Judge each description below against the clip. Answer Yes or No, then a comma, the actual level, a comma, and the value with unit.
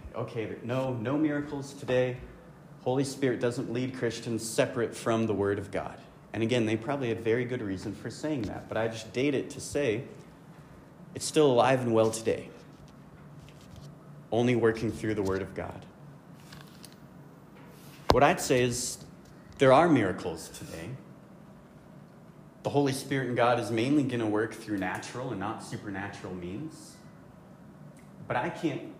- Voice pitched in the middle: No, low, 120 Hz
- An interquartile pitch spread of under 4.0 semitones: Yes, average, 3.6 semitones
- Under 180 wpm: Yes, average, 155 wpm